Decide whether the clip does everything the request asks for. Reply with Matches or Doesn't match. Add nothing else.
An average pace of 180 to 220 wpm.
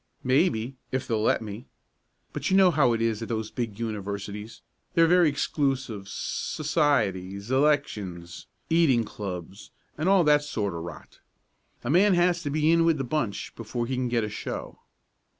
Doesn't match